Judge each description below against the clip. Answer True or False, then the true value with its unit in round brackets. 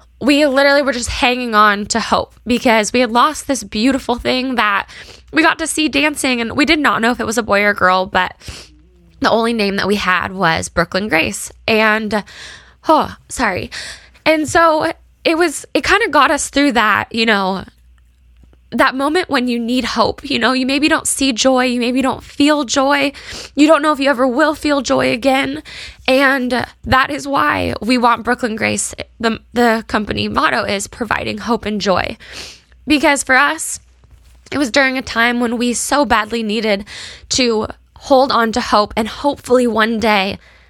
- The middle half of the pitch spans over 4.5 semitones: True (4.9 semitones)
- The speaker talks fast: False (185 wpm)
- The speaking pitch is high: True (245 Hz)